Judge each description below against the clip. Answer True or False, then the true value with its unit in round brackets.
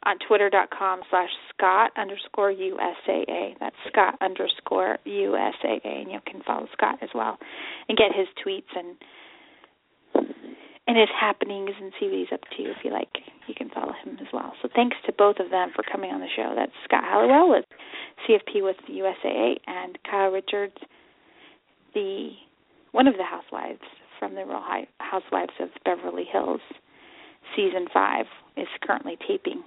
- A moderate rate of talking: True (160 wpm)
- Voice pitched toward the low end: False (225 Hz)